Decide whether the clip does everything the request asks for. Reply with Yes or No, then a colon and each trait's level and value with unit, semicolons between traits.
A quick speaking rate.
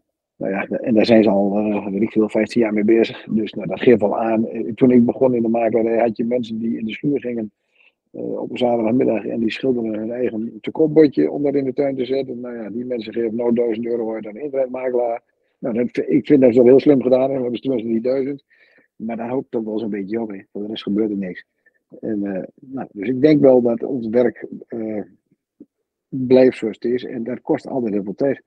Yes: fast, 240 wpm